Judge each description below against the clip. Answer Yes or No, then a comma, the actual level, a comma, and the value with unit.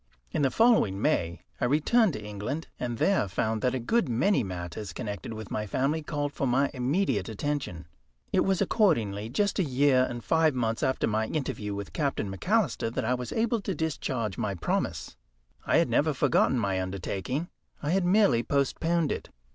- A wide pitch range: Yes, wide, 6.8 semitones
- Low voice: Yes, low, 130 Hz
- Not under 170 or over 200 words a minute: Yes, average, 180 wpm